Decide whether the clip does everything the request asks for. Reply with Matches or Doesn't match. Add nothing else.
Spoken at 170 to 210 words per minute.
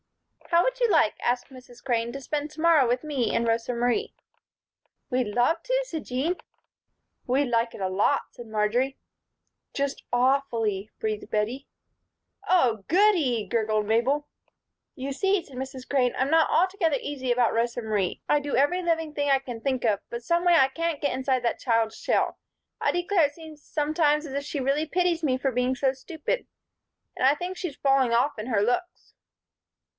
Matches